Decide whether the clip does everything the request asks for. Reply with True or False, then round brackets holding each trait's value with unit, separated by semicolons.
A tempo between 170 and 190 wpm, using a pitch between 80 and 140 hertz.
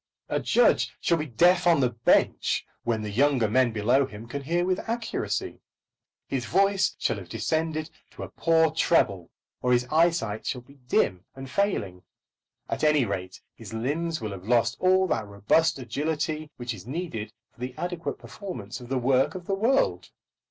True (175 wpm; 135 Hz)